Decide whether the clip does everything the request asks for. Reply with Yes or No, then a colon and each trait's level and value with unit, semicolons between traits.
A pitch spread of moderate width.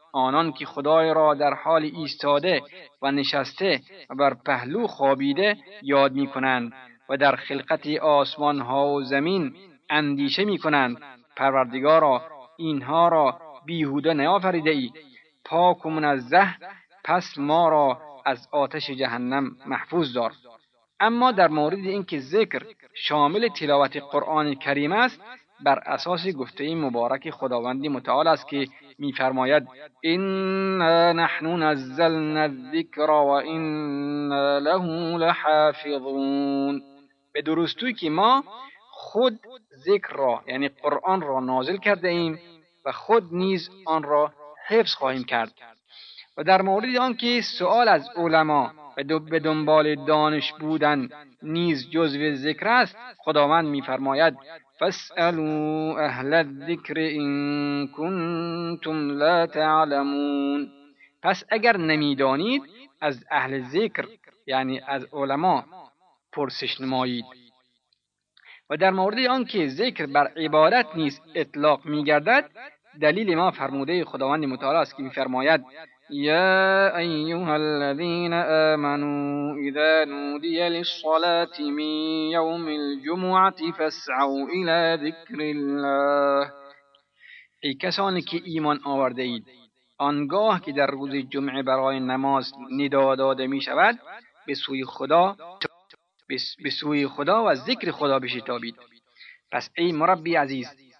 Yes: average, 3.2 semitones